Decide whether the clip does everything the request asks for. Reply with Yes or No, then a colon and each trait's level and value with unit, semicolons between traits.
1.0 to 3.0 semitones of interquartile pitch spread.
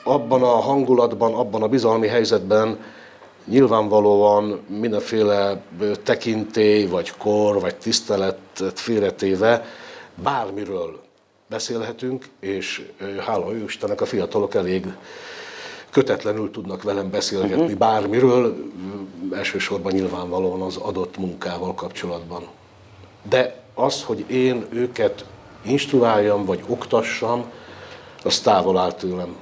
No: average, 4.2 semitones